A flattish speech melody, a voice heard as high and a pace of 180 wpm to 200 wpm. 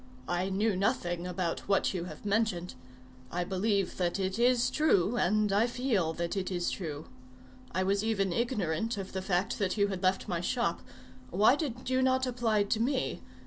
No: average, 4.3 semitones; high, 200 Hz; average, 185 wpm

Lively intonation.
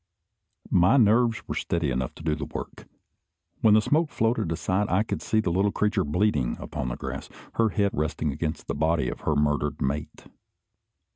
Yes: wide, 6.1 semitones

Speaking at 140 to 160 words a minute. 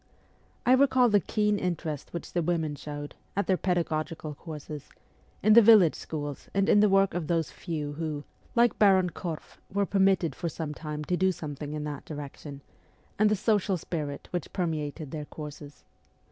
No: average, 175 wpm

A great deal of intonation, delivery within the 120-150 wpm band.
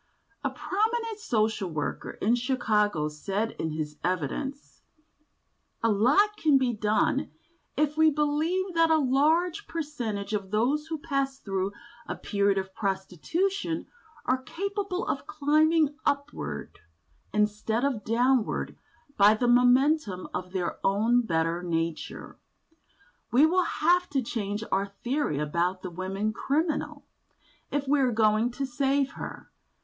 Yes: wide, 7.1 semitones; slow, 135 wpm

